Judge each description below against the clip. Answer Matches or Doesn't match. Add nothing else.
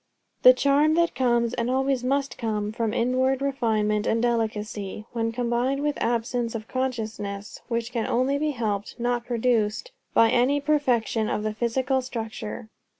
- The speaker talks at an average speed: Matches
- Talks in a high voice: Matches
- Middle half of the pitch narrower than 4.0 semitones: Matches